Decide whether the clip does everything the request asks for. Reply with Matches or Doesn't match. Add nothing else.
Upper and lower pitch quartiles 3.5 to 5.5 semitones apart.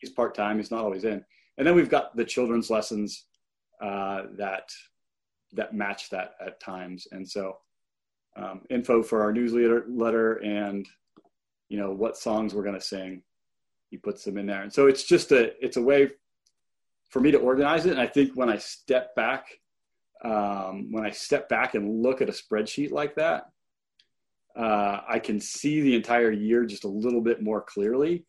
Doesn't match